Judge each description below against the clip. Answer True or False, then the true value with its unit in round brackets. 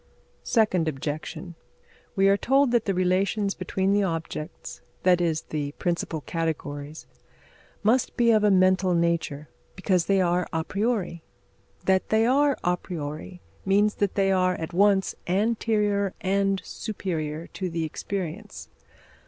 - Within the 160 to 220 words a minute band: False (135 wpm)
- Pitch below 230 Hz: True (185 Hz)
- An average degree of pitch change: True (3.4 semitones)